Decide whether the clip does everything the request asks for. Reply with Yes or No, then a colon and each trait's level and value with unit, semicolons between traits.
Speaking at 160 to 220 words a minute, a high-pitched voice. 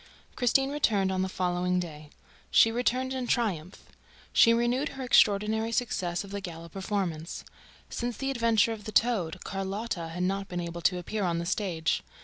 Yes: average, 170 wpm; high, 200 Hz